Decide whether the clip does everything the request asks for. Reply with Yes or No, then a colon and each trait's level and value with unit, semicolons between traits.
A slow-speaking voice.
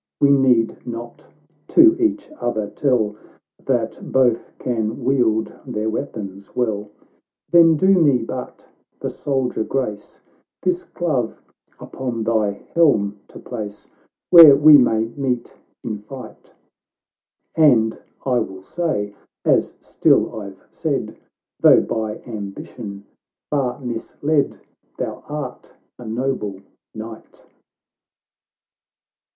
Yes: slow, 105 wpm